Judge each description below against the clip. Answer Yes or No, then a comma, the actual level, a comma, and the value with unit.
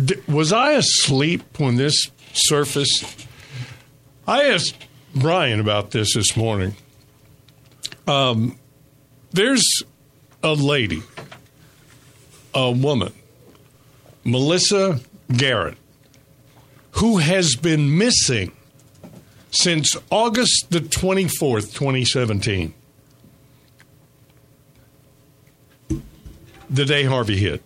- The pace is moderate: No, slow, 75 wpm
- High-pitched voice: No, low, 135 Hz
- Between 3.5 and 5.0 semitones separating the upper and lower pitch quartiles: No, narrow, 2.4 semitones